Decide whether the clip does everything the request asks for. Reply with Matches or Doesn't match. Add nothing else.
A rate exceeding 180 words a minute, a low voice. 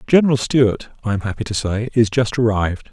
Matches